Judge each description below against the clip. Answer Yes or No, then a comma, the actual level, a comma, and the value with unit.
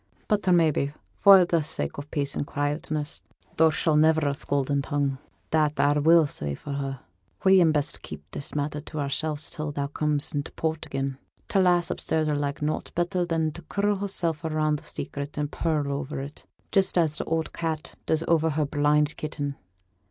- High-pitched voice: No, medium, 150 Hz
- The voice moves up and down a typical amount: No, narrow, 2.1 semitones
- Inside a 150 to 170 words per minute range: No, average, 190 wpm